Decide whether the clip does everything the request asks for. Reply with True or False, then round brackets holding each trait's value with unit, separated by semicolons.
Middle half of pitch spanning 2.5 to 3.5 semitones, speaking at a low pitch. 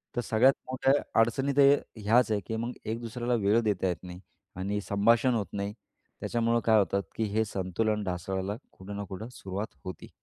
True (2.8 semitones; 110 Hz)